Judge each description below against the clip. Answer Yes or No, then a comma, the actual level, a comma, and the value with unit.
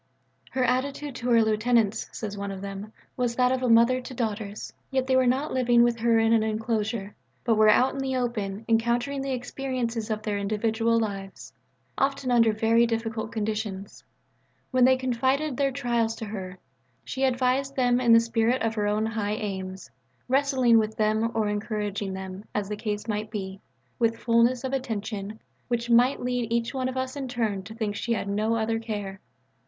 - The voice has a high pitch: Yes, high, 230 Hz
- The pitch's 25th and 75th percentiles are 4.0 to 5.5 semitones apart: No, average, 2.8 semitones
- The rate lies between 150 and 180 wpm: No, average, 190 wpm